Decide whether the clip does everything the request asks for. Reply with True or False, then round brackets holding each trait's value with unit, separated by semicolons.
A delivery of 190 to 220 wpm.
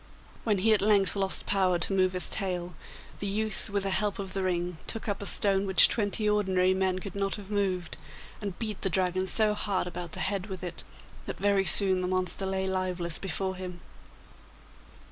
True (200 wpm)